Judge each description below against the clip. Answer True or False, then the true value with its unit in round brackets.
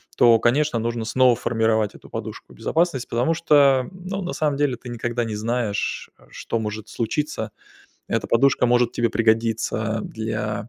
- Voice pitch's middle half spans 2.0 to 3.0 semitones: False (3.4 semitones)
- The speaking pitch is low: True (120 Hz)